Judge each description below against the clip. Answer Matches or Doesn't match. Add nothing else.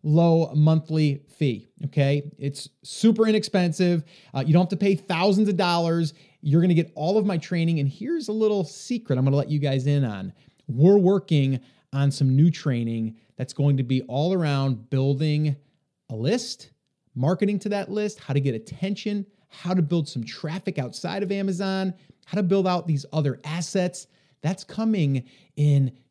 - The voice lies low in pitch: Doesn't match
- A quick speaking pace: Doesn't match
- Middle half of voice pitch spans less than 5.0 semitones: Doesn't match